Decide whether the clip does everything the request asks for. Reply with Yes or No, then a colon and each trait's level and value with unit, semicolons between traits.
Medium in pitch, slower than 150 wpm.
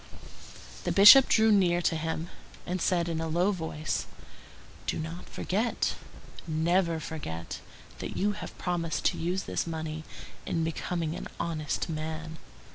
Yes: medium, 165 Hz; average, 140 wpm